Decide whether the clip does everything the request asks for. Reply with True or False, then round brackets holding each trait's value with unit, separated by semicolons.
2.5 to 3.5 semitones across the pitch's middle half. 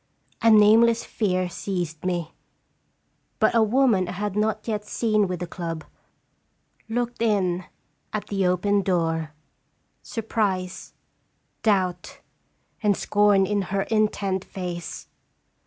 True (2.9 semitones)